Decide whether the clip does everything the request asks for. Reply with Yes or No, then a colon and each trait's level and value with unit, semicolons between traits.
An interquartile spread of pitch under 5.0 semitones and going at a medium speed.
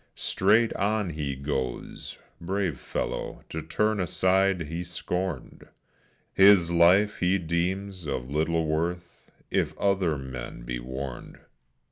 No: average, 4.4 semitones; slow, 115 wpm